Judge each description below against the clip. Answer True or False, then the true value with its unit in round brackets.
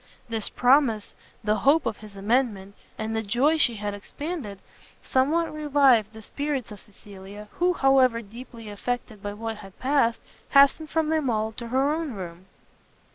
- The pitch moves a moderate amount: True (5.0 semitones)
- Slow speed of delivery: False (160 wpm)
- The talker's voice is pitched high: True (230 Hz)